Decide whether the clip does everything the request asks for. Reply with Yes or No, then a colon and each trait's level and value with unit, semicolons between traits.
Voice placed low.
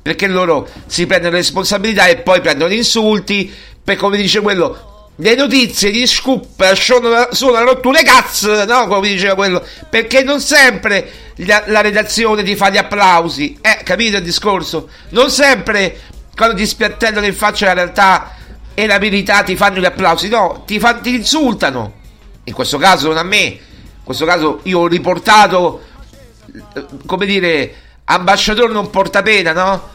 No: high, 200 Hz